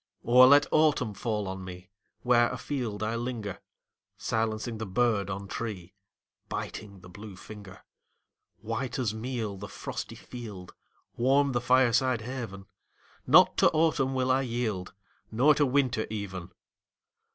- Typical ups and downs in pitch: Yes, average, 3.9 semitones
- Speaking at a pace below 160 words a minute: Yes, slow, 135 wpm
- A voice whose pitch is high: No, low, 115 Hz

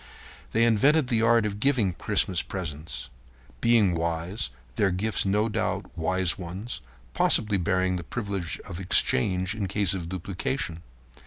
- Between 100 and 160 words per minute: Yes, average, 145 wpm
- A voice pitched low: Yes, very low, 95 Hz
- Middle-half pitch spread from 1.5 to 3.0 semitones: No, average, 3.9 semitones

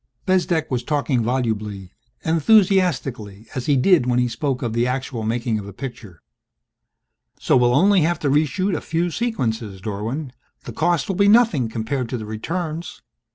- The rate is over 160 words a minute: Yes, average, 170 wpm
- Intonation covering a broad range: Yes, wide, 6.7 semitones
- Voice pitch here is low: Yes, low, 130 Hz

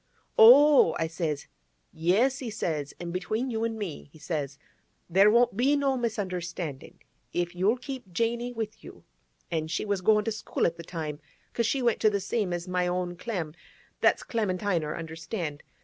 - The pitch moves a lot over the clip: Yes, wide, 5.7 semitones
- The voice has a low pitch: No, medium, 185 Hz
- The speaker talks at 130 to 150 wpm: No, average, 165 wpm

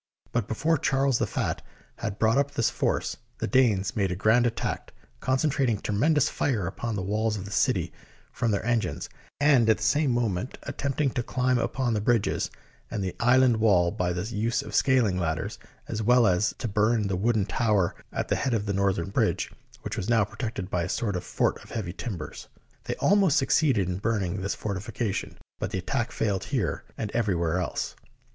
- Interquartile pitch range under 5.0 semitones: Yes, average, 4.1 semitones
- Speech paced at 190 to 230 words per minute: Yes, average, 200 wpm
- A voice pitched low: Yes, low, 110 Hz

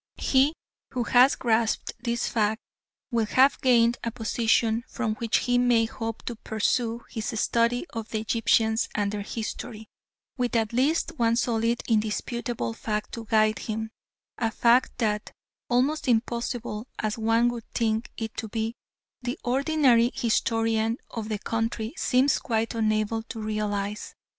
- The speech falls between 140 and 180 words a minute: Yes, average, 145 wpm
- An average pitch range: No, narrow, 1.7 semitones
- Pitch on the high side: Yes, high, 230 Hz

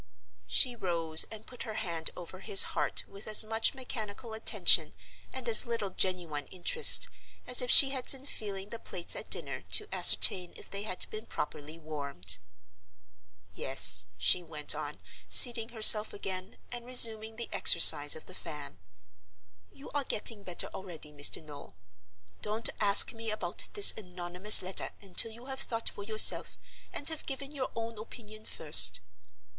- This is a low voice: No, high, 200 Hz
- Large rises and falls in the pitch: Yes, wide, 6.2 semitones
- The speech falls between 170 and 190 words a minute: No, average, 155 wpm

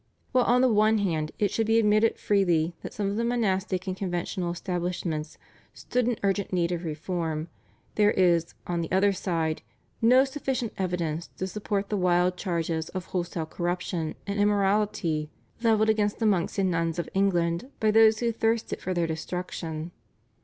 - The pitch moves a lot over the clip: No, average, 3.8 semitones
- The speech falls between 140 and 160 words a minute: No, average, 170 wpm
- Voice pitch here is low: No, medium, 185 Hz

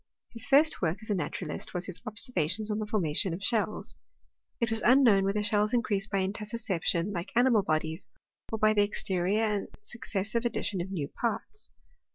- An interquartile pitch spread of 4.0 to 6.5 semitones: No, average, 3.1 semitones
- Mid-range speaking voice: No, high, 210 Hz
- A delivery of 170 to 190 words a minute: Yes, average, 175 wpm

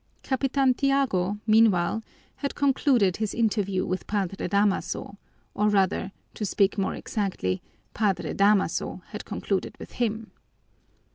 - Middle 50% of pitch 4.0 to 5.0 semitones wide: No, average, 3.0 semitones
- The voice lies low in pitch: No, high, 205 Hz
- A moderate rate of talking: No, slow, 120 wpm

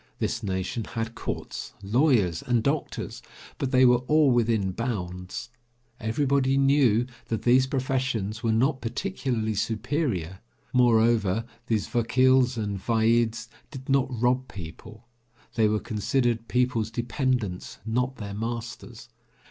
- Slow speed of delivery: Yes, slow, 120 wpm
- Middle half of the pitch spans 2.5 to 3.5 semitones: Yes, average, 2.9 semitones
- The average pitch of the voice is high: No, low, 115 Hz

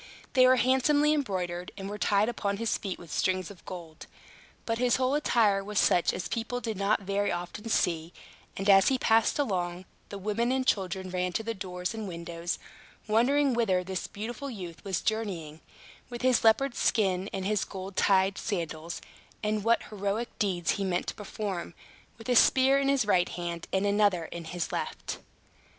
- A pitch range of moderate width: Yes, average, 4.1 semitones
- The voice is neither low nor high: No, high, 200 Hz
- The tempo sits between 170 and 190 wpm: Yes, average, 180 wpm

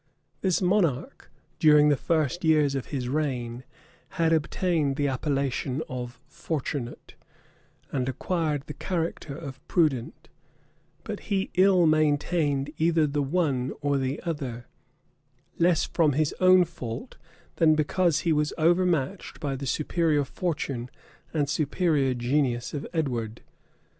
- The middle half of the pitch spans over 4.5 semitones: No, average, 3.6 semitones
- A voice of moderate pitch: Yes, medium, 150 Hz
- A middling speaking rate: No, slow, 125 wpm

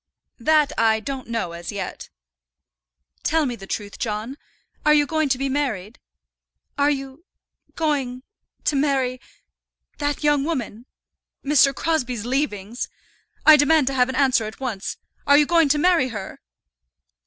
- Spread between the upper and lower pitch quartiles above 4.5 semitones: No, average, 4.1 semitones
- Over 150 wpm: No, average, 145 wpm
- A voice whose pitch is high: Yes, very high, 270 Hz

